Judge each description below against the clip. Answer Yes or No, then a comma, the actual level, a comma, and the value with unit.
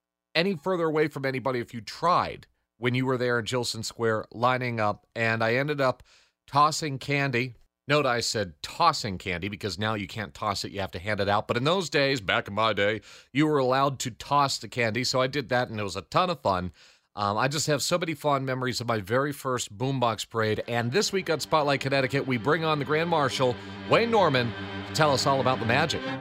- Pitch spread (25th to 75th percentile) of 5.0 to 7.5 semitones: No, average, 4.6 semitones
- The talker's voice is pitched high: No, low, 125 Hz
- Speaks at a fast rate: Yes, fast, 230 wpm